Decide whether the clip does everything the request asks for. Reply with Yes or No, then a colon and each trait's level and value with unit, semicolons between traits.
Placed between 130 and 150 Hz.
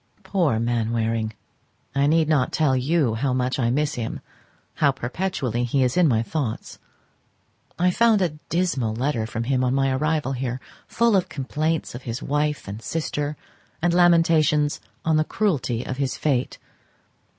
Yes: medium, 140 Hz